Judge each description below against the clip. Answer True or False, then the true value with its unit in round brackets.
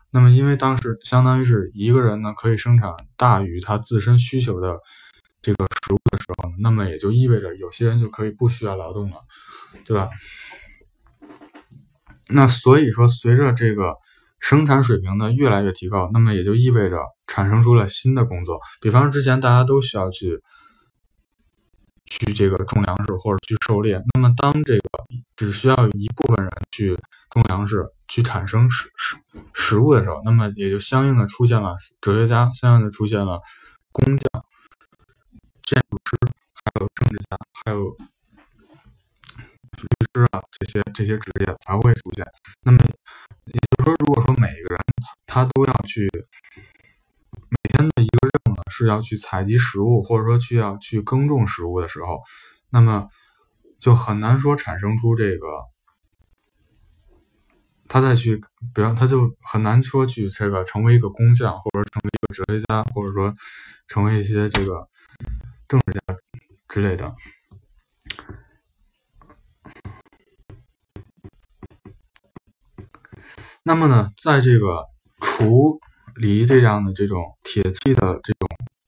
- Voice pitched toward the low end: True (110 Hz)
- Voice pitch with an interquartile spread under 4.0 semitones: True (3.4 semitones)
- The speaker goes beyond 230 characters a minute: False (220 characters per minute)